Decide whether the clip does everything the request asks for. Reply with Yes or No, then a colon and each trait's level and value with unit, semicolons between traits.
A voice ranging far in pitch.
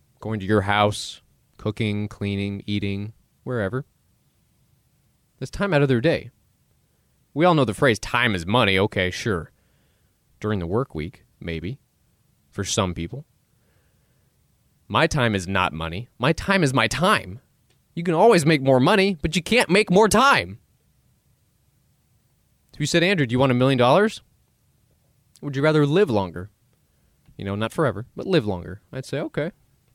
Yes: wide, 6.7 semitones